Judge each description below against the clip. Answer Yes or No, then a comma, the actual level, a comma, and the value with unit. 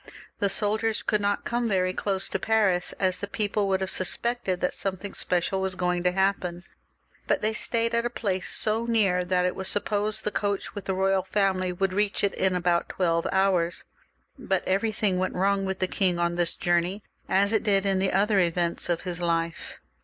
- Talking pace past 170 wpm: Yes, average, 200 wpm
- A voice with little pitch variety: Yes, narrow, 2.2 semitones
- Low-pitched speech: No, high, 190 Hz